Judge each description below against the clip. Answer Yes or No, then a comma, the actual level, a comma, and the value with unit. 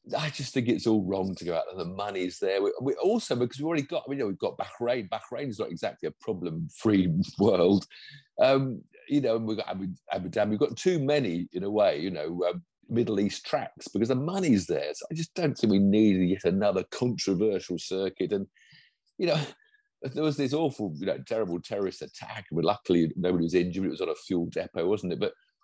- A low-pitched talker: Yes, low, 115 Hz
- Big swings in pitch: Yes, wide, 8.4 semitones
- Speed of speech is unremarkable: No, fast, 240 wpm